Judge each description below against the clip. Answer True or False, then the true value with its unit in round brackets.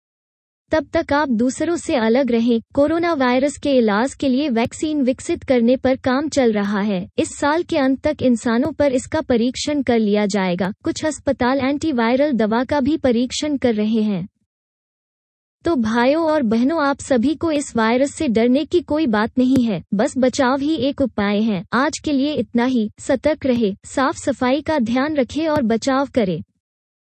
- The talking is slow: False (175 wpm)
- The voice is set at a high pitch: True (265 Hz)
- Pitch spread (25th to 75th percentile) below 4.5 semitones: True (4.1 semitones)